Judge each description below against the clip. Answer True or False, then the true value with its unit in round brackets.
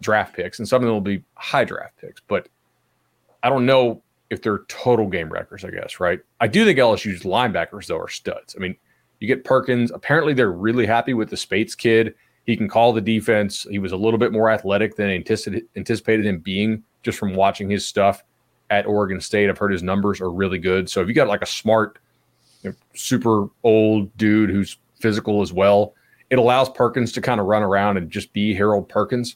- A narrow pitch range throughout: True (2.3 semitones)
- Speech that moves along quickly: True (210 wpm)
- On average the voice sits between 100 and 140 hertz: True (105 Hz)